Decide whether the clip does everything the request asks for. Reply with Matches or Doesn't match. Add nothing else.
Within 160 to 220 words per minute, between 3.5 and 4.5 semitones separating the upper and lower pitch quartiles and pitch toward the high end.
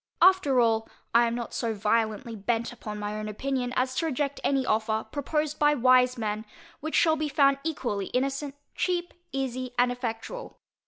Matches